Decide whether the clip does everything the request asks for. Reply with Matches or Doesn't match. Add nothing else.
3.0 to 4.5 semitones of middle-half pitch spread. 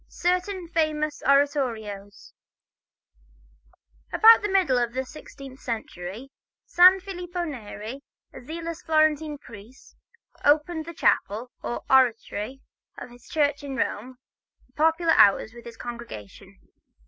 Doesn't match